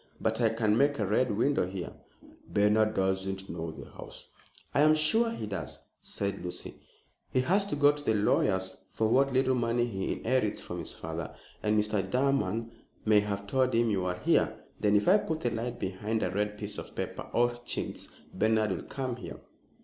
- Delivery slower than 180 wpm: No, average, 195 wpm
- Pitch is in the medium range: No, low, 110 Hz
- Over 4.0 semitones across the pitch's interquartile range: Yes, average, 4.4 semitones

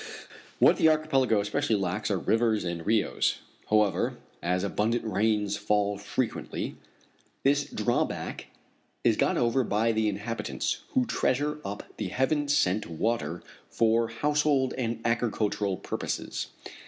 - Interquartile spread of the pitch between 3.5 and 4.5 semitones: Yes, average, 4.0 semitones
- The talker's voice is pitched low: Yes, low, 110 Hz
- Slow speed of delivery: Yes, slow, 125 wpm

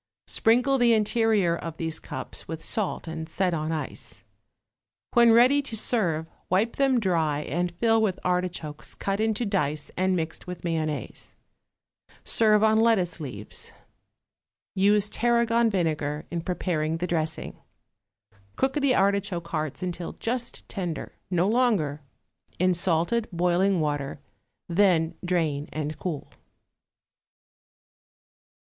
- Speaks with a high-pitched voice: No, medium, 180 Hz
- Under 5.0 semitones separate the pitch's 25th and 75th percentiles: No, average, 5.3 semitones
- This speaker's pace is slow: Yes, slow, 120 wpm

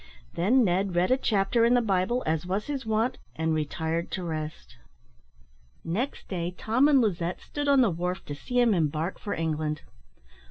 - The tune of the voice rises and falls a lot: Yes, wide, 6.5 semitones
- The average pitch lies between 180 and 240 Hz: Yes, medium, 185 Hz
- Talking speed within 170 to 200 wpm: Yes, average, 175 wpm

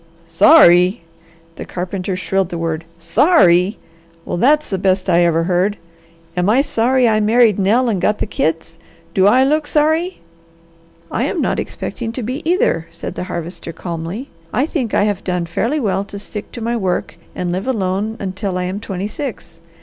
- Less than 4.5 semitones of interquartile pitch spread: No, average, 5.0 semitones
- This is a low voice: No, high, 195 Hz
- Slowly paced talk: No, average, 180 wpm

